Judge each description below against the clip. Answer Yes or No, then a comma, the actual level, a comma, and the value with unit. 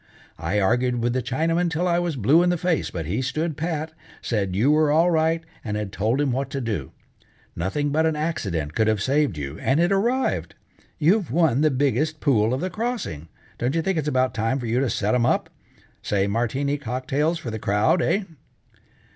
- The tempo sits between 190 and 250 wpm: Yes, fast, 205 wpm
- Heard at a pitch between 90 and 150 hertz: Yes, low, 135 Hz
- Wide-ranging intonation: Yes, wide, 6.5 semitones